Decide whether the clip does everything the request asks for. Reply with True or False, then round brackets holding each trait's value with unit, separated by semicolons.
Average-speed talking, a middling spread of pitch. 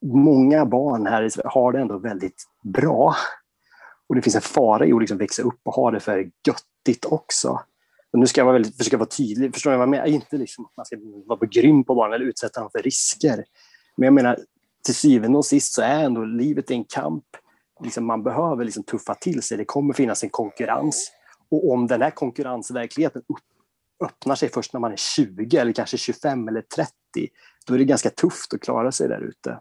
False (215 wpm; 3.5 semitones)